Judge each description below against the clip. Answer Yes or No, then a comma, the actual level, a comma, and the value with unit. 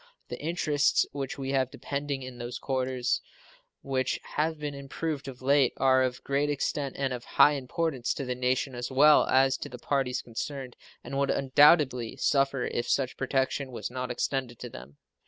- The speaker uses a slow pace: No, average, 180 wpm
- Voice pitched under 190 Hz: Yes, low, 135 Hz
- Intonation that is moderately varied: No, narrow, 1.9 semitones